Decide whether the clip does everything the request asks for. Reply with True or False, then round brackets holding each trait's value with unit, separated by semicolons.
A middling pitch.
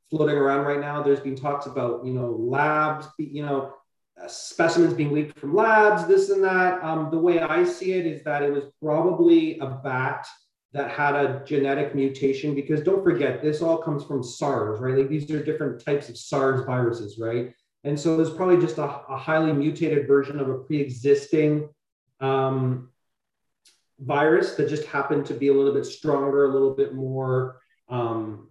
True (145 Hz)